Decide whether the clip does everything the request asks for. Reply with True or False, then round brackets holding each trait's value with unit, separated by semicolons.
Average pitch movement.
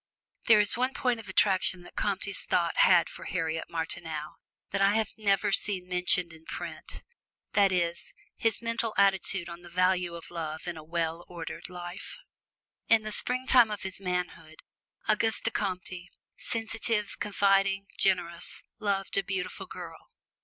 True (3.1 semitones)